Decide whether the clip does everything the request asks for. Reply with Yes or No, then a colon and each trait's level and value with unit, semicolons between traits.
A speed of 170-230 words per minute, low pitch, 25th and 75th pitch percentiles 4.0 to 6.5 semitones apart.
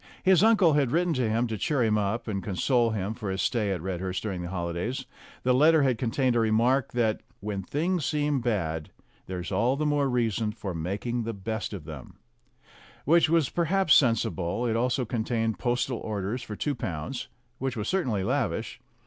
Yes: average, 190 wpm; low, 115 Hz; average, 4.8 semitones